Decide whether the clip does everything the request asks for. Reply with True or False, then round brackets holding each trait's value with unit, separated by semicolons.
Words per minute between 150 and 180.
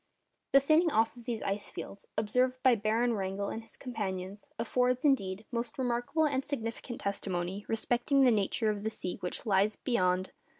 True (170 wpm)